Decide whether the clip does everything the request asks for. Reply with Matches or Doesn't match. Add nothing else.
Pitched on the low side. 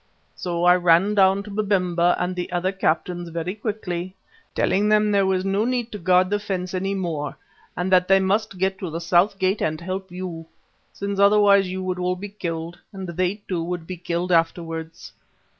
Doesn't match